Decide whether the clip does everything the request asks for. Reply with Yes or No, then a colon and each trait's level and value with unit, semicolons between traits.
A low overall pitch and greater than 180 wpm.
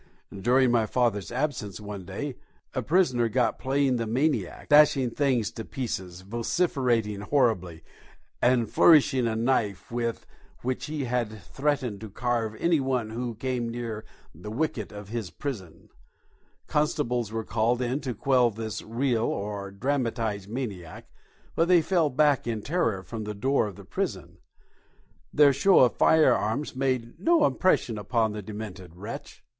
No: low, 120 Hz; average, 150 wpm